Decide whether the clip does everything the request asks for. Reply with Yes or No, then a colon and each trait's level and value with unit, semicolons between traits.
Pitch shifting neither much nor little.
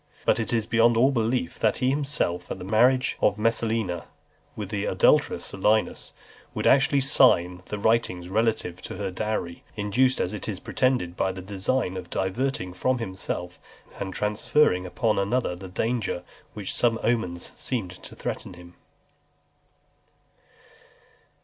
Yes: average, 4.5 semitones